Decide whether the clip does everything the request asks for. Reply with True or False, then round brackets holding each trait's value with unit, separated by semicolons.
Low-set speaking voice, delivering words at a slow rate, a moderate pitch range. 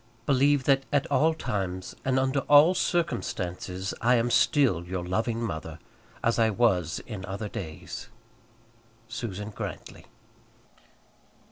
False (115 Hz; 120 wpm; 6.4 semitones)